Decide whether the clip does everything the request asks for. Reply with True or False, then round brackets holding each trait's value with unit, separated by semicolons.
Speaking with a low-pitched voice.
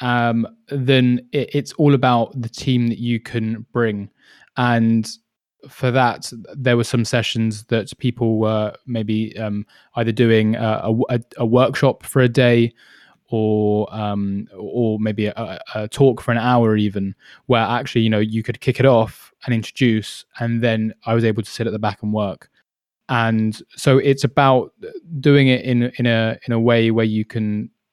True (115 Hz)